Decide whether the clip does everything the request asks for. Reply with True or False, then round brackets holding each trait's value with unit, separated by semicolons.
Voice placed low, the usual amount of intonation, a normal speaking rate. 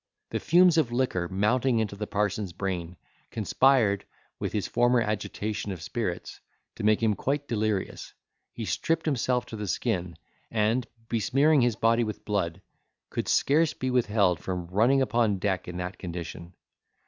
True (110 Hz; 4.5 semitones; 160 wpm)